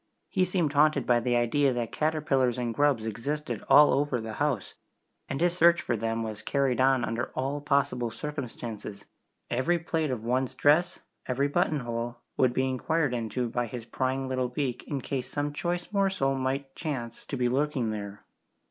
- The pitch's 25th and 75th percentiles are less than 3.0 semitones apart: No, average, 3.5 semitones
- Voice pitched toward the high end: No, low, 130 Hz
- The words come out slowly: No, average, 175 wpm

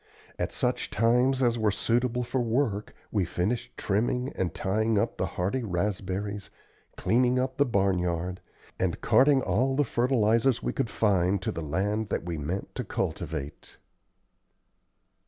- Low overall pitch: Yes, low, 110 Hz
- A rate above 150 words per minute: No, average, 145 wpm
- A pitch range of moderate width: Yes, average, 4.7 semitones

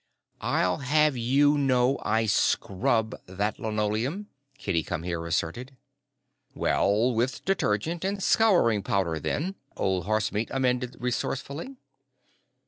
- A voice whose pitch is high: No, low, 120 Hz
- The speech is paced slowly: Yes, slow, 110 wpm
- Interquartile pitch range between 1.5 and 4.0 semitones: No, average, 5.3 semitones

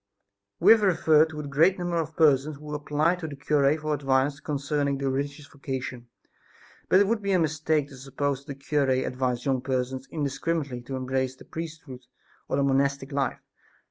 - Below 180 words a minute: No, average, 185 wpm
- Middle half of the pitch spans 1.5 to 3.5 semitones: Yes, narrow, 2.6 semitones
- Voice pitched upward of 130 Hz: Yes, medium, 140 Hz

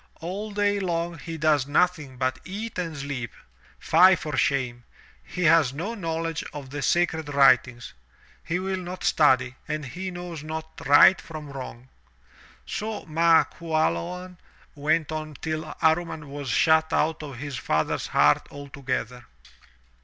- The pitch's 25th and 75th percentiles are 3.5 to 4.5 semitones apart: Yes, average, 3.9 semitones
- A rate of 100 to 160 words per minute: Yes, average, 140 wpm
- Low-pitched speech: No, medium, 155 Hz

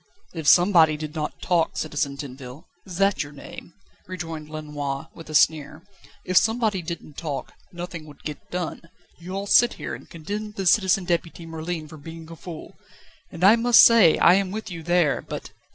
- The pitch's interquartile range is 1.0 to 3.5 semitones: Yes, average, 3.2 semitones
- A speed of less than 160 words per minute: No, average, 185 wpm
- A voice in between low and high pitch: Yes, medium, 165 Hz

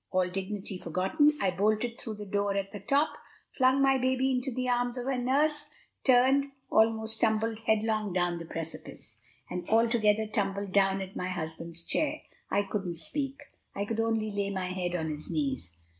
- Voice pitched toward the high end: Yes, high, 210 Hz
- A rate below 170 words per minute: No, average, 175 wpm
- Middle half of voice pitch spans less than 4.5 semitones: No, average, 4.9 semitones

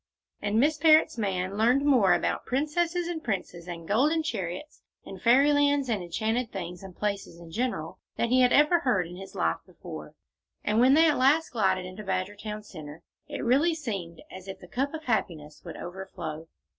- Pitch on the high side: Yes, high, 215 Hz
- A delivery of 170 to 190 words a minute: Yes, average, 180 wpm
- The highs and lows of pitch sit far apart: Yes, wide, 7.4 semitones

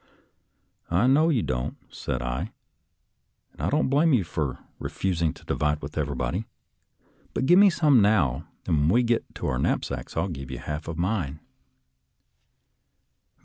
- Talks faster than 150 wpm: Yes, average, 165 wpm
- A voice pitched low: Yes, very low, 85 Hz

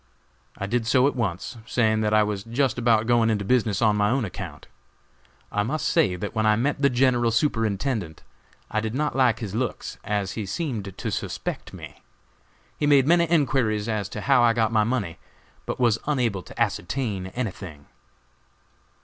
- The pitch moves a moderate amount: Yes, average, 3.6 semitones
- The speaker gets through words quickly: No, average, 180 wpm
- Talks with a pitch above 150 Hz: No, low, 115 Hz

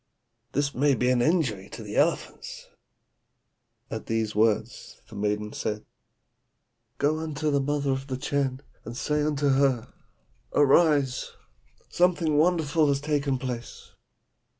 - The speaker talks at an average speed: No, slow, 125 wpm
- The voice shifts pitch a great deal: No, average, 3.6 semitones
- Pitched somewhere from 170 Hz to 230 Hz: No, medium, 140 Hz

